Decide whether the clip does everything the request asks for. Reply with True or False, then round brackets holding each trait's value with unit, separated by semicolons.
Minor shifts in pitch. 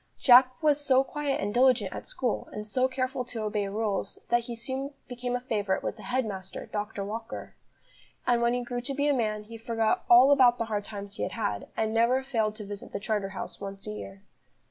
False (3.6 semitones)